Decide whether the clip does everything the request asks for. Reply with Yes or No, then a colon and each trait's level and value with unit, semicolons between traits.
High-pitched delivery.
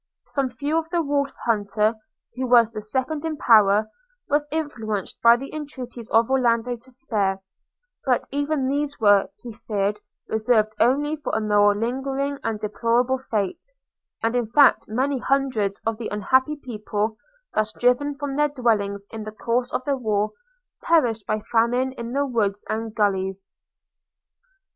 Yes: high, 235 Hz